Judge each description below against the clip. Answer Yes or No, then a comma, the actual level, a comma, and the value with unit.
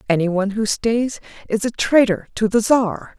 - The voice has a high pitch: Yes, high, 215 Hz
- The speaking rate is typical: Yes, average, 170 wpm